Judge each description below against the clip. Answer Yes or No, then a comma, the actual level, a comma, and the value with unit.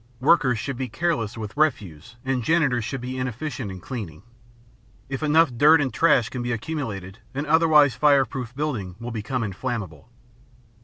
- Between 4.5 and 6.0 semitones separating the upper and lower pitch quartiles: Yes, average, 5.0 semitones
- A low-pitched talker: Yes, low, 125 Hz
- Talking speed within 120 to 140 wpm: No, average, 155 wpm